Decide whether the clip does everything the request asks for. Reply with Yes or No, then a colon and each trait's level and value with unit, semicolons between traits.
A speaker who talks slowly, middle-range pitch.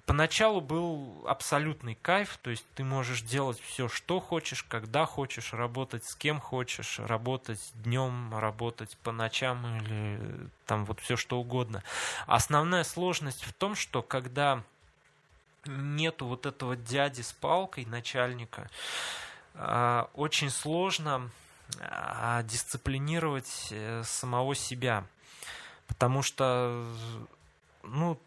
No: slow, 105 wpm; low, 125 Hz